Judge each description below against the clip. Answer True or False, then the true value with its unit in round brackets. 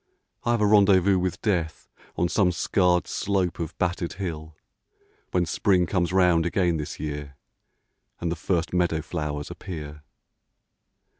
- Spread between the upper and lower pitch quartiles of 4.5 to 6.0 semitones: False (2.7 semitones)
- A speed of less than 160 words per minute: True (140 wpm)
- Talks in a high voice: False (90 Hz)